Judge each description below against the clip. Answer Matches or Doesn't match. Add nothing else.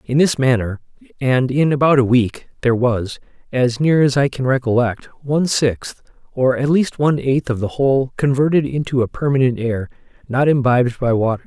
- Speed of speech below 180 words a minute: Doesn't match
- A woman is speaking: Doesn't match